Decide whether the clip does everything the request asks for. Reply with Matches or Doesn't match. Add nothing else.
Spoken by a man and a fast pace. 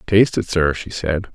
Matches